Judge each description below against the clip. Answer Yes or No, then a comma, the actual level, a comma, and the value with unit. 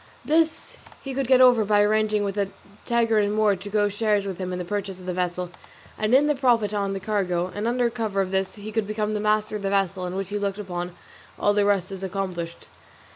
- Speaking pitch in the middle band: No, high, 205 Hz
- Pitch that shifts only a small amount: Yes, narrow, 2.1 semitones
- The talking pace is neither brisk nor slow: No, fast, 240 wpm